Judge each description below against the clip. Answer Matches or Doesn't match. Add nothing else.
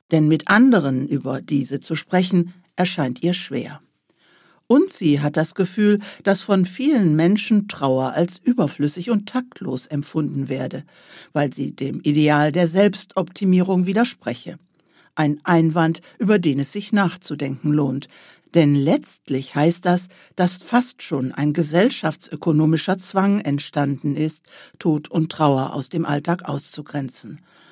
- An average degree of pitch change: Matches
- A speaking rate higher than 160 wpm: Doesn't match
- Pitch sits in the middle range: Matches